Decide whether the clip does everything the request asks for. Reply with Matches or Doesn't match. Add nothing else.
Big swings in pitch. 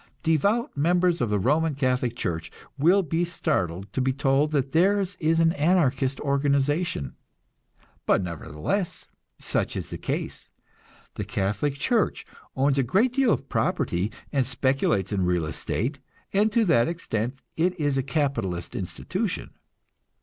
Matches